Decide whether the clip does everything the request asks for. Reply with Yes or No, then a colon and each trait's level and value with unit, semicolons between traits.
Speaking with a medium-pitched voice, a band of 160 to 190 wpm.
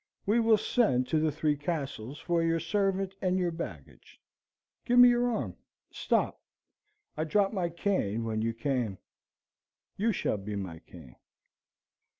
No: medium, 165 Hz; average, 150 wpm